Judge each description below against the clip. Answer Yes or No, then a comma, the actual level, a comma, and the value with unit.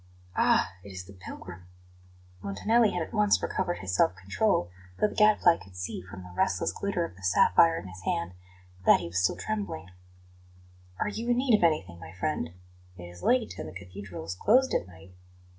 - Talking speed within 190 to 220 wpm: Yes, average, 195 wpm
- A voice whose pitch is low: Yes, very low, 95 Hz